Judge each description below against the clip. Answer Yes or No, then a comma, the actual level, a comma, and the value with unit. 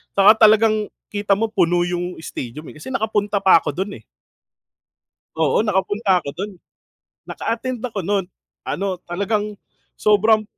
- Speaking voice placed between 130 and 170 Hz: No, high, 200 Hz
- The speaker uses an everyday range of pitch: Yes, average, 3.3 semitones